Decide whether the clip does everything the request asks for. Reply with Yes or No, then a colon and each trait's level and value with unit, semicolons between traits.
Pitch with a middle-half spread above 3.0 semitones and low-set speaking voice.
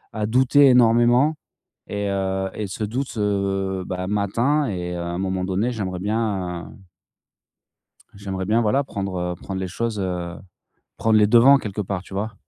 Yes: average, 3.4 semitones; low, 100 Hz